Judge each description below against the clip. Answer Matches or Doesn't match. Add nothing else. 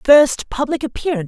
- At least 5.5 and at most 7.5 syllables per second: Matches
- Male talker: Doesn't match